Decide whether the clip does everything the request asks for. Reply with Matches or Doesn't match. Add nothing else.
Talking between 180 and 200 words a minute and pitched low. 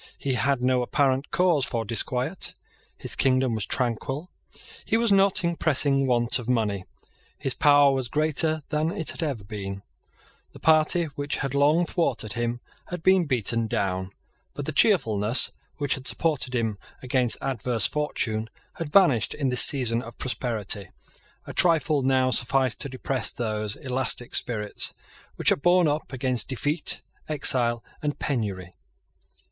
Doesn't match